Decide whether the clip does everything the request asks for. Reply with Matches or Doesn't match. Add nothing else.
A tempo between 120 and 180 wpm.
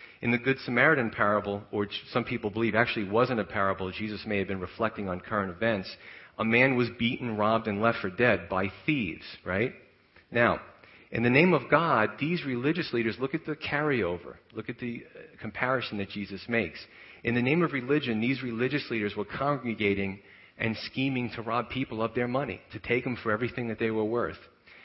Doesn't match